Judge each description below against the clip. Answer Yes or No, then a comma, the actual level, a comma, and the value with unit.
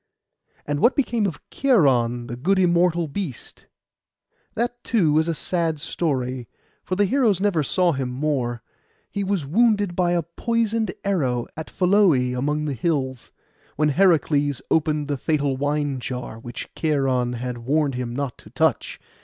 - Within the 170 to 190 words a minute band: No, average, 155 wpm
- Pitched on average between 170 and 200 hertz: No, medium, 150 Hz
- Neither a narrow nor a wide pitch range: No, wide, 6.0 semitones